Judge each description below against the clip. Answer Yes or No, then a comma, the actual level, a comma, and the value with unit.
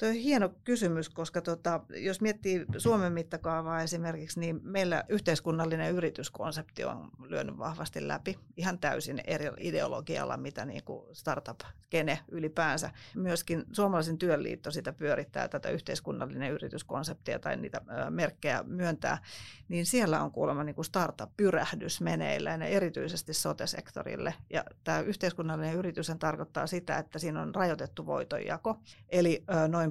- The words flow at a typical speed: Yes, average, 125 wpm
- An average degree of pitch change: No, narrow, 2.3 semitones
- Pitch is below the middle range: No, medium, 165 Hz